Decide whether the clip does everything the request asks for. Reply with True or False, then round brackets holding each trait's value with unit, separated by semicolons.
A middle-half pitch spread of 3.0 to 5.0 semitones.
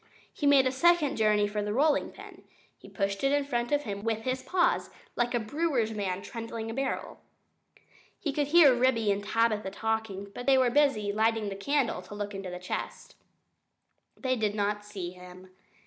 True (4.7 semitones)